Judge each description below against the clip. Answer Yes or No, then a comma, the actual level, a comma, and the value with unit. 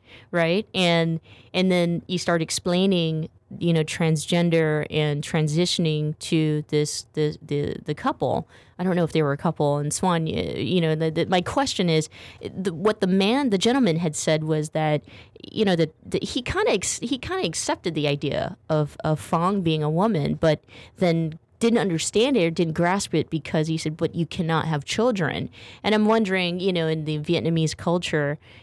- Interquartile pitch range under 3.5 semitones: Yes, average, 3.0 semitones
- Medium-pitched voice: Yes, medium, 165 Hz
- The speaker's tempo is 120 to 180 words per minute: No, average, 195 wpm